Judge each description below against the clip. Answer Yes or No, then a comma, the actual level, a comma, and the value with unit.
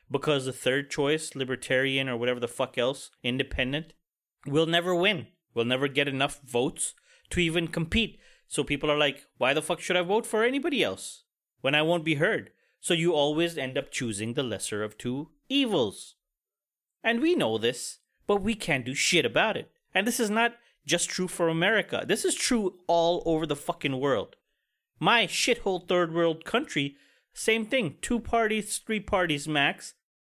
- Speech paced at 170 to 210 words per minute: Yes, average, 180 wpm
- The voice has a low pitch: No, medium, 160 Hz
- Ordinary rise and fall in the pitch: No, wide, 6.5 semitones